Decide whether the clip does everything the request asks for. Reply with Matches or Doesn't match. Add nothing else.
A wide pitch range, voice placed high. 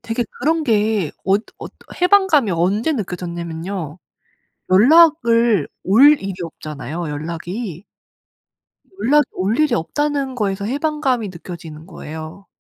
Matches